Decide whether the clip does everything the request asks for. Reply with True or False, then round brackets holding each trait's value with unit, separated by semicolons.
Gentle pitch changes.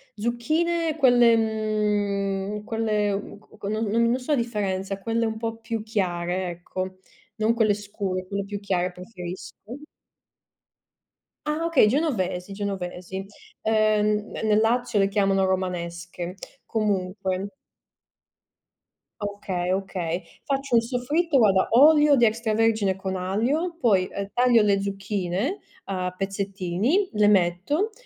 False (3.5 semitones)